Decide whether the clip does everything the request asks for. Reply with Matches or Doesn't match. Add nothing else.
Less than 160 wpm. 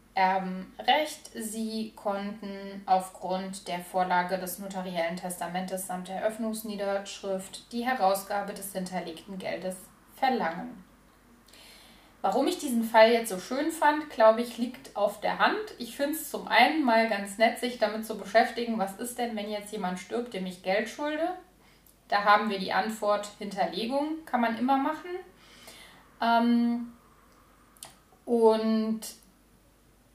Matches